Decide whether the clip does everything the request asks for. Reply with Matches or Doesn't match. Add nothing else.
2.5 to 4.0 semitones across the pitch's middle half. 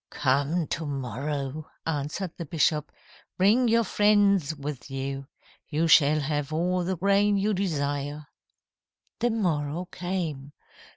Doesn't match